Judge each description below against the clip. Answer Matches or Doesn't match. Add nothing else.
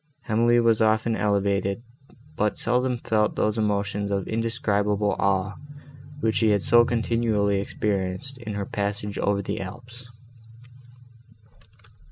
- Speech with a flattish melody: Matches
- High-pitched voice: Doesn't match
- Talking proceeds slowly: Matches